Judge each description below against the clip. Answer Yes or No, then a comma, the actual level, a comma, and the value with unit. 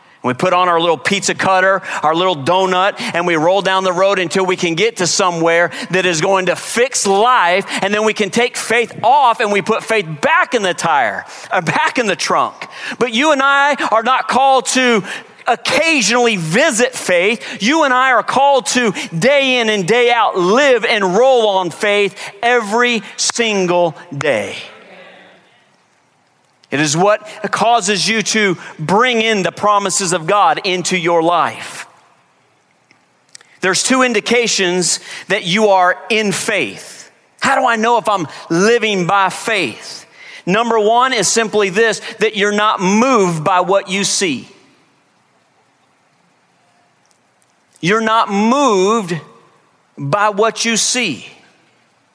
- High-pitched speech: Yes, high, 210 Hz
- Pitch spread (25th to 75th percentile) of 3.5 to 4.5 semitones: Yes, average, 4.2 semitones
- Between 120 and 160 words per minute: Yes, average, 150 wpm